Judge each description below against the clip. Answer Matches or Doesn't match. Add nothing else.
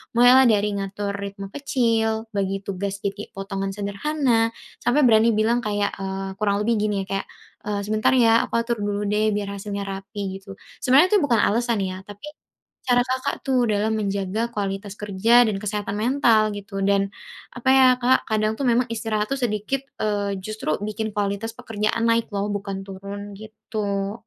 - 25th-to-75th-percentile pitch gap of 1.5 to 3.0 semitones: Matches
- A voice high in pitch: Matches